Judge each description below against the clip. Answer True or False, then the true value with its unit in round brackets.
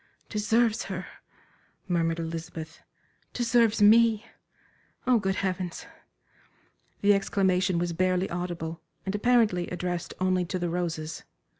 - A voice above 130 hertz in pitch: True (185 Hz)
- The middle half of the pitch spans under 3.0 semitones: False (3.3 semitones)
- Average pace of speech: False (110 wpm)